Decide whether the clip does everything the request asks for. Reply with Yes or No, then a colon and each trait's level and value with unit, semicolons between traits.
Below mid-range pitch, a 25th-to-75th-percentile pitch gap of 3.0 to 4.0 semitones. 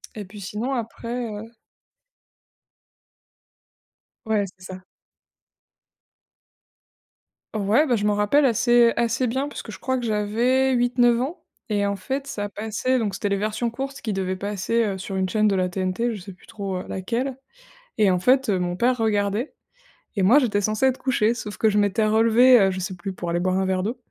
No: high, 215 Hz; average, 3.7 semitones